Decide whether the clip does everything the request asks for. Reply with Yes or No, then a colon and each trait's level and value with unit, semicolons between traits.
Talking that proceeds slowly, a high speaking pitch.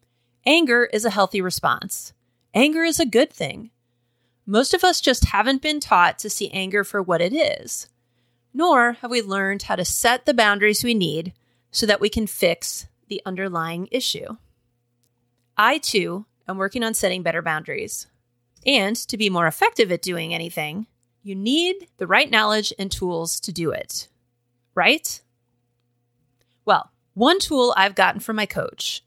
No: average, 160 wpm; high, 195 Hz